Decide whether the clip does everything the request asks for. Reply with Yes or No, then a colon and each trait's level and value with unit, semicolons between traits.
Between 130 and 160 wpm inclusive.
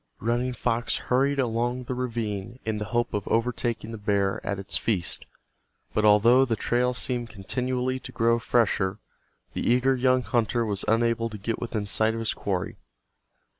No: average, 170 wpm